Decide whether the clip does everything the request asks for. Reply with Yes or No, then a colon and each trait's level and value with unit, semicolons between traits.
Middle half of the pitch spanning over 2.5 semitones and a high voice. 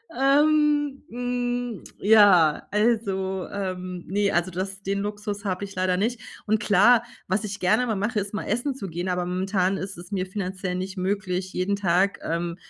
Yes: average, 2.9 semitones; high, 200 Hz